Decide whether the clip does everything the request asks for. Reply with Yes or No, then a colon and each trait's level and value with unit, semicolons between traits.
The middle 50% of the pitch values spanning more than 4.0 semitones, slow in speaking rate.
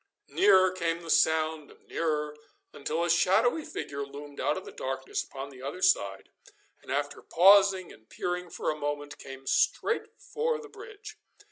No: average, 4.8 semitones; average, 165 wpm